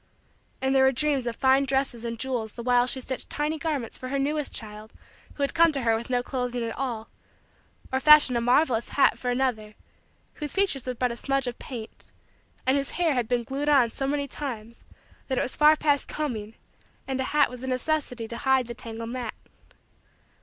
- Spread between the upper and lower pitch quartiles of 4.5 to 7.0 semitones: No, average, 2.9 semitones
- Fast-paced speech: Yes, fast, 210 wpm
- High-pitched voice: Yes, very high, 255 Hz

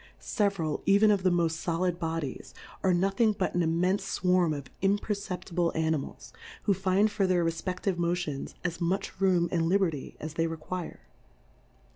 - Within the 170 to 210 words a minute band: No, average, 160 wpm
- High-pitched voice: No, medium, 180 Hz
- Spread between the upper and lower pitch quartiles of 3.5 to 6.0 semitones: No, average, 2.9 semitones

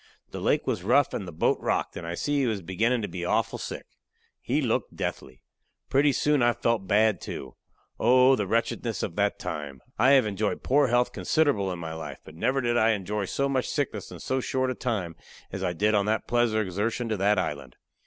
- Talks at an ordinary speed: No, fast, 215 wpm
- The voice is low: Yes, low, 110 Hz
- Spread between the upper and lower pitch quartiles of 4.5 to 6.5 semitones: Yes, average, 5.1 semitones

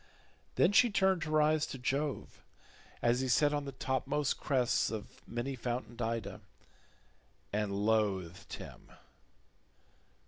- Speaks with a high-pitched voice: No, low, 130 Hz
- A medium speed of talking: No, slow, 125 wpm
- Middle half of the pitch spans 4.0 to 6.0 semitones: Yes, average, 4.8 semitones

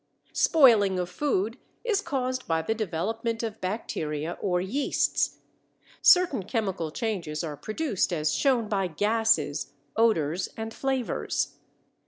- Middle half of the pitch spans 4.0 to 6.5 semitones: Yes, average, 5.2 semitones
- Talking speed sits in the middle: No, slow, 120 wpm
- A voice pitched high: Yes, high, 215 Hz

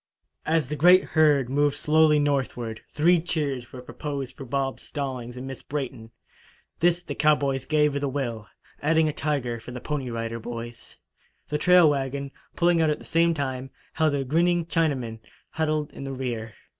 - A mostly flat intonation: No, average, 3.5 semitones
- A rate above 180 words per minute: No, average, 175 wpm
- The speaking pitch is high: No, medium, 140 Hz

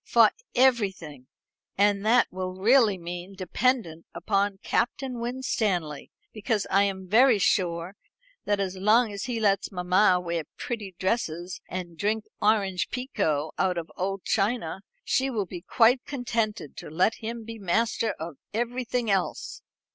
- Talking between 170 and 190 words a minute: No, average, 140 wpm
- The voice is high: Yes, high, 200 Hz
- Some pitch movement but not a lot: Yes, average, 4.2 semitones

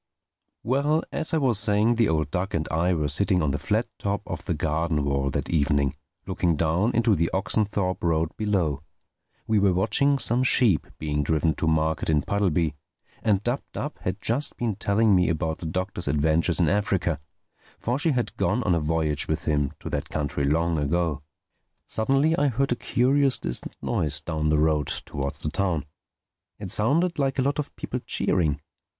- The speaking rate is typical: Yes, average, 185 wpm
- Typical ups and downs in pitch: No, wide, 6.3 semitones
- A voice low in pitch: Yes, very low, 90 Hz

